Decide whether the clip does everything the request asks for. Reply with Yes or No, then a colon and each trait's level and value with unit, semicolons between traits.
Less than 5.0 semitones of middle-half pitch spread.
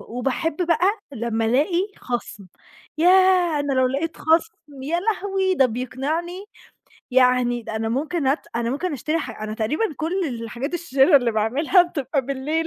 No: wide, 5.5 semitones